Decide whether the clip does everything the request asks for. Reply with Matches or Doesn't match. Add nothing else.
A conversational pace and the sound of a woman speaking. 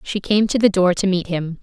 Doesn't match